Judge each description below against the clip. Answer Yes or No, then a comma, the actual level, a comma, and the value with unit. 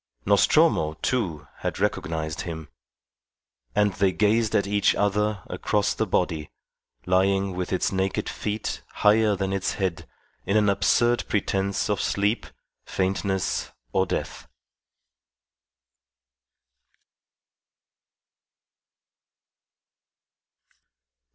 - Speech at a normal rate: No, slow, 90 wpm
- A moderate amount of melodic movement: No, narrow, 2.1 semitones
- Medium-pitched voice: No, very low, 95 Hz